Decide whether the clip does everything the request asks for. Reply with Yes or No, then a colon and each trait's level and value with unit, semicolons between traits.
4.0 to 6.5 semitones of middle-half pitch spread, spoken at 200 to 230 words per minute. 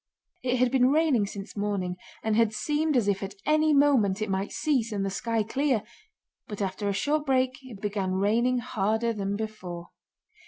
No: average, 4.4 semitones; average, 185 wpm